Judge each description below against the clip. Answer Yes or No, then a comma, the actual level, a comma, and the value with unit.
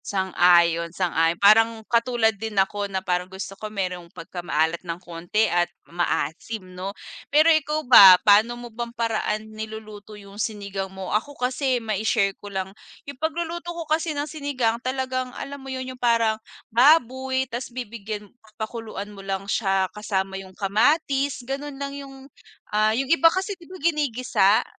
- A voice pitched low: No, high, 220 Hz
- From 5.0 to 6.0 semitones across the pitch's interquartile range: Yes, average, 5.3 semitones